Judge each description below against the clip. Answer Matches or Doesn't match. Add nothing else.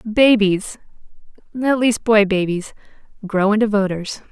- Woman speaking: Matches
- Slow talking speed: Matches